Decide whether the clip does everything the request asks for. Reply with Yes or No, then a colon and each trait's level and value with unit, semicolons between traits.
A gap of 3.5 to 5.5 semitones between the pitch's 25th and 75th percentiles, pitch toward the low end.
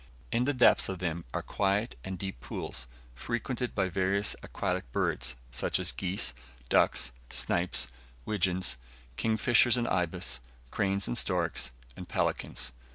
Yes: average, 4.4 semitones; very low, 95 Hz